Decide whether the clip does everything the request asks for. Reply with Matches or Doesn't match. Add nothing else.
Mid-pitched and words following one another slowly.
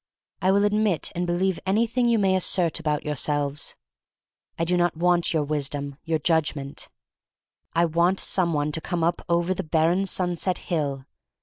Doesn't match